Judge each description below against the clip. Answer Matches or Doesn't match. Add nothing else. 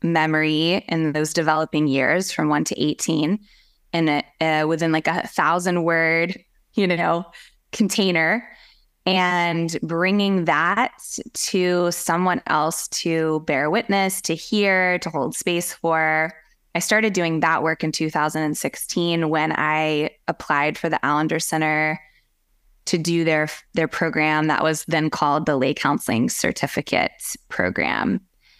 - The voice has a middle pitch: Matches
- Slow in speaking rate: Matches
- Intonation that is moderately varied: Doesn't match